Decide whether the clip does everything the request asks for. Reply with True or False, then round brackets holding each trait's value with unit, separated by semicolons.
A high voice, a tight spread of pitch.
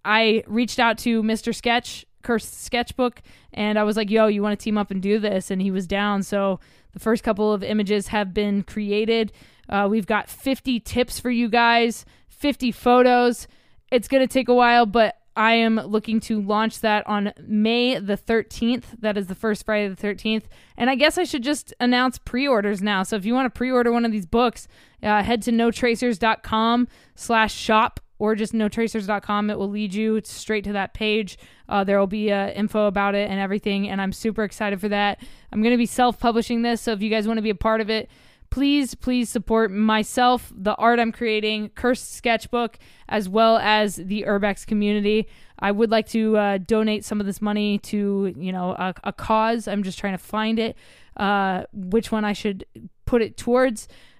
True (220 Hz; 2.2 semitones)